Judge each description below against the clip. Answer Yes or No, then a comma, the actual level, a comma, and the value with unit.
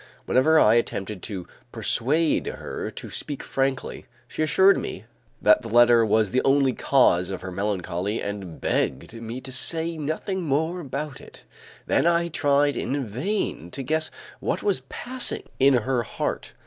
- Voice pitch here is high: No, low, 130 Hz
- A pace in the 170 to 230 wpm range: No, average, 160 wpm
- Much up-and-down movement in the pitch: Yes, wide, 6.6 semitones